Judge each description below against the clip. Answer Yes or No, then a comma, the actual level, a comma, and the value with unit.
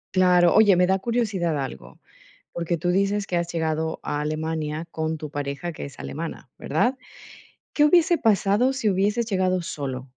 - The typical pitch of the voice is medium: Yes, medium, 175 Hz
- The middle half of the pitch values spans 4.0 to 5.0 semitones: Yes, average, 4.6 semitones